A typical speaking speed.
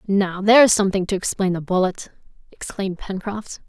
Yes: average, 145 wpm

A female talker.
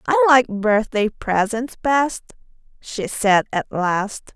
Yes: female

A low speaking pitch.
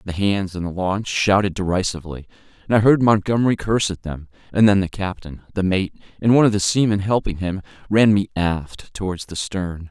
Yes: very low, 95 Hz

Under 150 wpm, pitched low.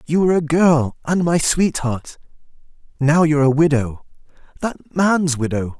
No: slow, 135 wpm; medium, 150 Hz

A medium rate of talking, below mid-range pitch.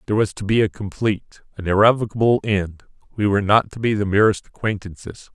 Yes: average, 190 wpm; low, 100 Hz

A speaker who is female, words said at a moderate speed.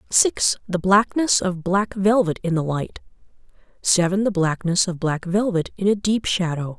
Yes: female; average, 170 wpm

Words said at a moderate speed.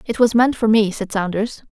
No: fast, 245 wpm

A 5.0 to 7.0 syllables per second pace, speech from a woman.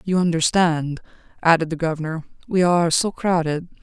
Yes: 5.4 syllables/s; female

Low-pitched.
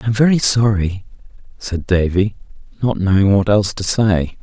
Yes: low, 100 Hz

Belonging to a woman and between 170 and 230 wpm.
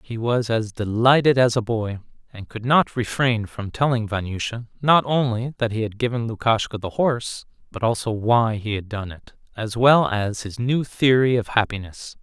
No: male; average, 185 wpm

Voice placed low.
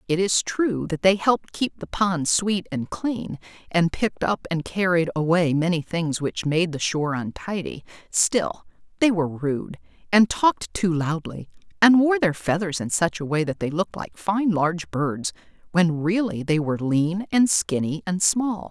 No: medium, 170 Hz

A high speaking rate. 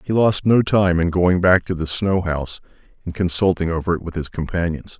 Yes: fast, 215 wpm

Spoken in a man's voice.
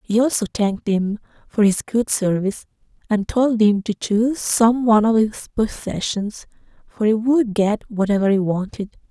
No: female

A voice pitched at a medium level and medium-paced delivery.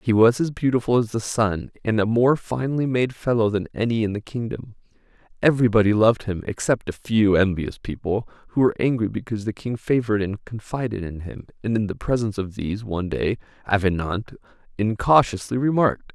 No: low, 110 Hz; average, 180 wpm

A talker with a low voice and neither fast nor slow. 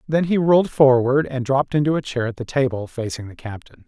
No: low, 130 Hz; fast, 230 wpm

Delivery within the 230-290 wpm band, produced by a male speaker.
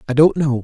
Yes: fast, 285 wpm; male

